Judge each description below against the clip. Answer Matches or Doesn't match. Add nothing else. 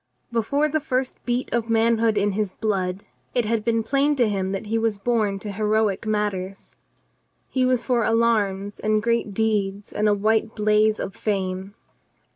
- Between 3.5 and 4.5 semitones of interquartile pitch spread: Doesn't match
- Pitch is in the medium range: Doesn't match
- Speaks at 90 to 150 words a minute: Doesn't match